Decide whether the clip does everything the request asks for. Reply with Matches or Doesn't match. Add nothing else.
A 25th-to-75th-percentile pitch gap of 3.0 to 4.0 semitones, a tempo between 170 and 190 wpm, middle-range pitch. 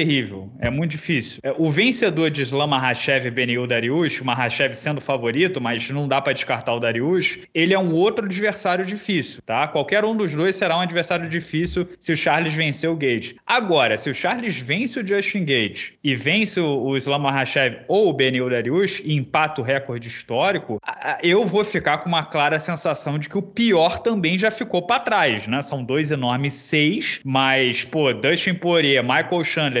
Doesn't match